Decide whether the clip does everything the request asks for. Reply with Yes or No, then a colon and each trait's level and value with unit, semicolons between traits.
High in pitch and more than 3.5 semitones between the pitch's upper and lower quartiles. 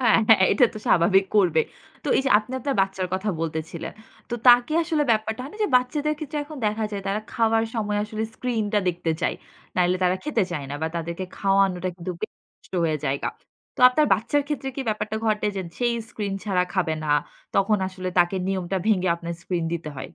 Yes: high, 200 Hz; average, 4.3 semitones